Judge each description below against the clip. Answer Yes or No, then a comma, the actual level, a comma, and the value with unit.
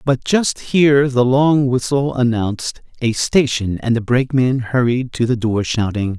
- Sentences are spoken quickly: No, average, 165 wpm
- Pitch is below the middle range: Yes, low, 125 Hz